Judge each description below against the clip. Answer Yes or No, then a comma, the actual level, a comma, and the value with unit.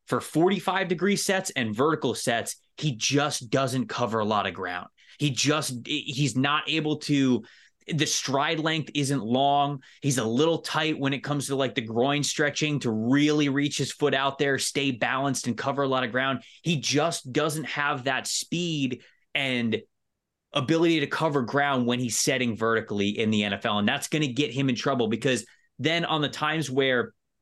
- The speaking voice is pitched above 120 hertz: Yes, medium, 140 Hz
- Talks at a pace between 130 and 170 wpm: No, average, 185 wpm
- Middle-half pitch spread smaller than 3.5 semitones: Yes, average, 3.1 semitones